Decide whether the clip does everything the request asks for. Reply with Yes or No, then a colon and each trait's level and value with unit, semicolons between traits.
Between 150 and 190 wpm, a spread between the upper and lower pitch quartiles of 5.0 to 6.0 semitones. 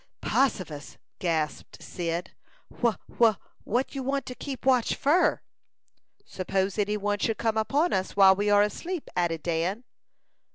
No: average, 140 wpm; wide, 5.5 semitones